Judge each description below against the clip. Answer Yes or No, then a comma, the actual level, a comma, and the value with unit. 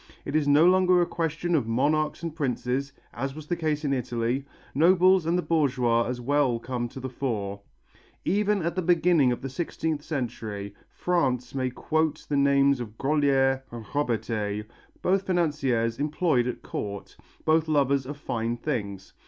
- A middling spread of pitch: Yes, average, 4.7 semitones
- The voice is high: No, medium, 140 Hz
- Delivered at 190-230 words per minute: No, average, 165 wpm